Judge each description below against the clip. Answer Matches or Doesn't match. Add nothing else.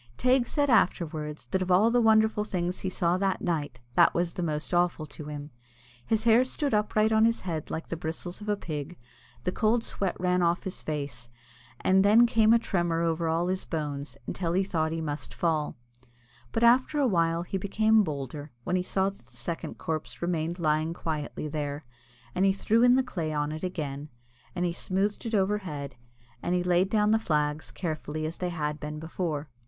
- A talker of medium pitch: Matches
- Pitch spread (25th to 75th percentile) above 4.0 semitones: Matches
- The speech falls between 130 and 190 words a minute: Doesn't match